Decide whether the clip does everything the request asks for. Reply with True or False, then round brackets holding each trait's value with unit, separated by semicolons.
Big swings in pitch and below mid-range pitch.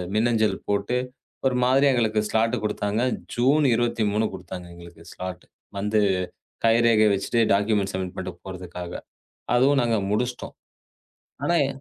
False (4.0 semitones; 110 Hz)